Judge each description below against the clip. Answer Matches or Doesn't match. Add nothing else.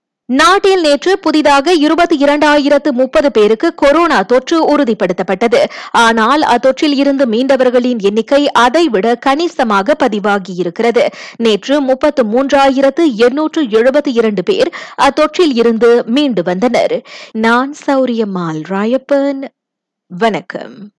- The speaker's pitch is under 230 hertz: Doesn't match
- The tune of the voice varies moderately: Matches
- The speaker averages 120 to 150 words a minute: Doesn't match